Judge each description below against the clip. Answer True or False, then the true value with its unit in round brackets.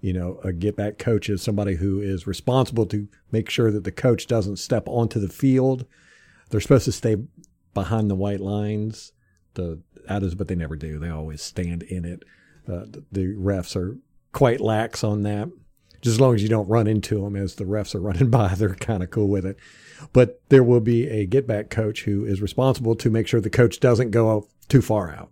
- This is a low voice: True (105 Hz)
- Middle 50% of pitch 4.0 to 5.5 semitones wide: False (3.0 semitones)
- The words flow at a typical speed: False (215 wpm)